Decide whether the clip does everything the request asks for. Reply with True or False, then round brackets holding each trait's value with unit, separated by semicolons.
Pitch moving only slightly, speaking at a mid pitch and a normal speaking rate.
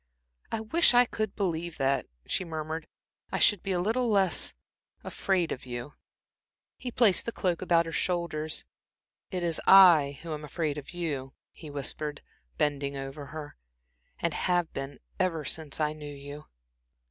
False (4.0 semitones; 160 Hz; 160 wpm)